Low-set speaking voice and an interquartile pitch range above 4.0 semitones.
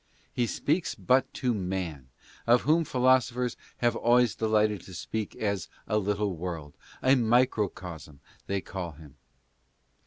Yes: low, 105 Hz; average, 5.3 semitones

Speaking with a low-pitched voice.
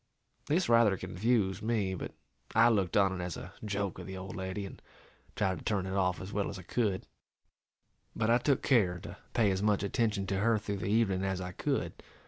Yes: low, 100 Hz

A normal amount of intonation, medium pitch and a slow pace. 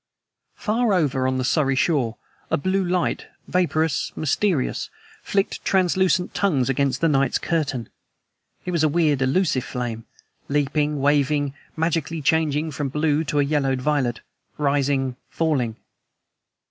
Yes: average, 3.4 semitones; medium, 145 Hz; slow, 130 wpm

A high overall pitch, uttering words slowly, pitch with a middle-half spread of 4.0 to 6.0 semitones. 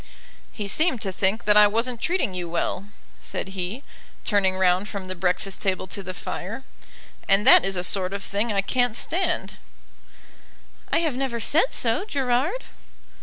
No: high, 205 Hz; average, 170 wpm; average, 4.6 semitones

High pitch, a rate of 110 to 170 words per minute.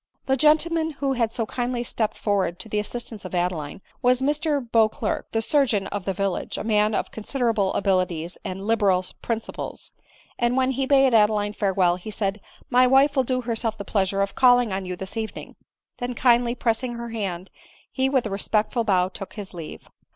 No: high, 220 Hz; average, 195 wpm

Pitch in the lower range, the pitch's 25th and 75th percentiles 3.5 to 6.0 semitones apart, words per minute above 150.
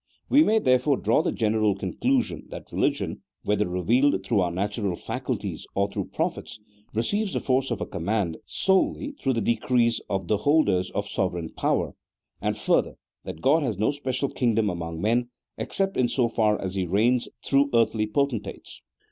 Yes: low, 115 Hz; average, 5.0 semitones; average, 175 wpm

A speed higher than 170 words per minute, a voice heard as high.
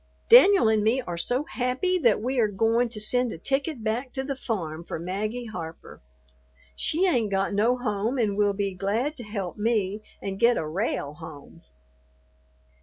Yes: average, 180 wpm; high, 220 Hz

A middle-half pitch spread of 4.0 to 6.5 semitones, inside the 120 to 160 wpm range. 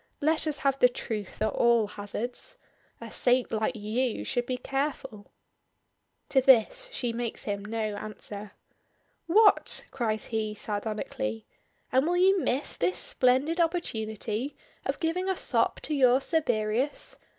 Yes: average, 5.1 semitones; average, 140 wpm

